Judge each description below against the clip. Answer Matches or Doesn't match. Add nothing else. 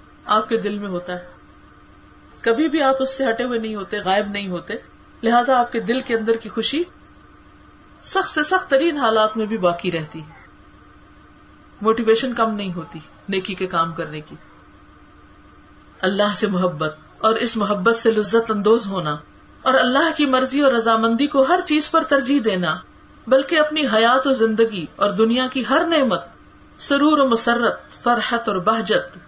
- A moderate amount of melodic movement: Doesn't match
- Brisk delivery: Doesn't match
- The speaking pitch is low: Doesn't match